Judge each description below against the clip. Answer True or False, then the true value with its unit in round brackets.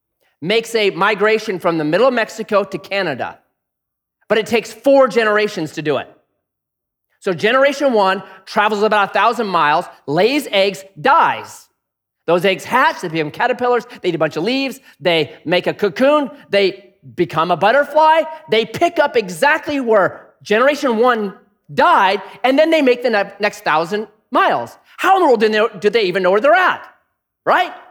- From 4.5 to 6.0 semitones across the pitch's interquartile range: True (4.9 semitones)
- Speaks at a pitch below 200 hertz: False (210 Hz)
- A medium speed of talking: True (165 wpm)